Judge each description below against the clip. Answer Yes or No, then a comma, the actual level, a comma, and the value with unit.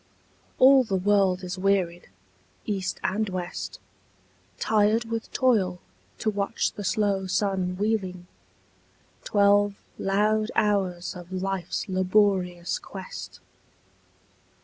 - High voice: Yes, high, 195 Hz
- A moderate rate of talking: No, slow, 100 wpm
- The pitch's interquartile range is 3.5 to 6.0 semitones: No, narrow, 2.4 semitones